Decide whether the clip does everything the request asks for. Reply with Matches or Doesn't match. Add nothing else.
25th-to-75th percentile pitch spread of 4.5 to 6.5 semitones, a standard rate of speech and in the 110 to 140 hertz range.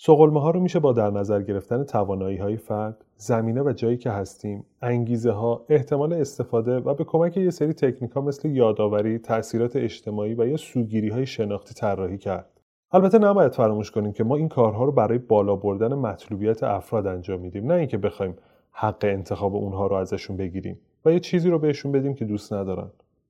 Doesn't match